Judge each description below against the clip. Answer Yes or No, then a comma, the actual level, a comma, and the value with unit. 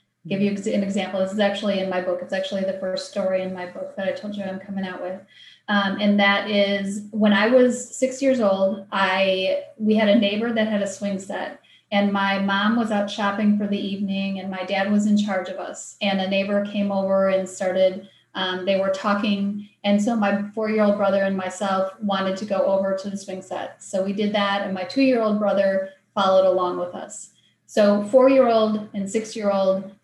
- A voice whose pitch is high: Yes, high, 200 Hz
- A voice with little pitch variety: Yes, narrow, 1.4 semitones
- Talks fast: Yes, fast, 210 wpm